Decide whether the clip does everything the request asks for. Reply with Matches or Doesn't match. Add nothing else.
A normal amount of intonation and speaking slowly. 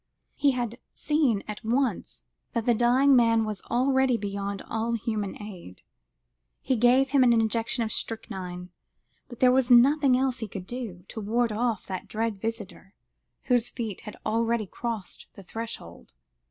Doesn't match